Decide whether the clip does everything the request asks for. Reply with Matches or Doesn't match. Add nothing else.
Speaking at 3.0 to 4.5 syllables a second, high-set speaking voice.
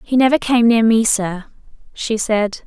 Matches